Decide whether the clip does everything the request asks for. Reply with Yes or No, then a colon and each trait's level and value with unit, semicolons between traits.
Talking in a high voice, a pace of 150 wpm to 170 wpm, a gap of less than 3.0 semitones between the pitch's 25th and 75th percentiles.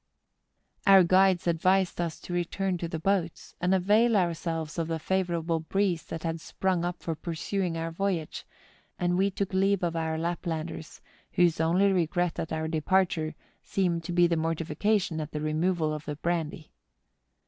No: medium, 170 Hz; average, 165 wpm; narrow, 2.5 semitones